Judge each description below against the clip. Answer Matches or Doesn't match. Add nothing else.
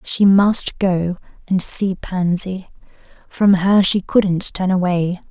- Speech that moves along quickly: Doesn't match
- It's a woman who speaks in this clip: Matches